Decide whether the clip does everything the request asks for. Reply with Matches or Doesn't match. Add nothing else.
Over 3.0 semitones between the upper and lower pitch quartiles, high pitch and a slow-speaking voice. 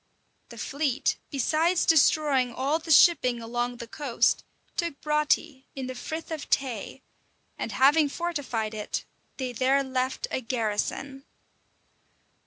Matches